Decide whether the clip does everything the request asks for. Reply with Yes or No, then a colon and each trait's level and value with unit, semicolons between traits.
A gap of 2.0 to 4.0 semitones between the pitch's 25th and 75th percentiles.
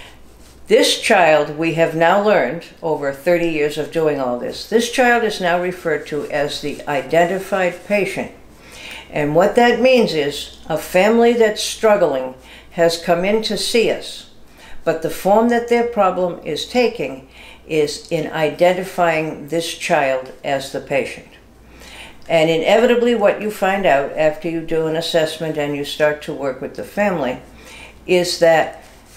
No: average, 4.7 semitones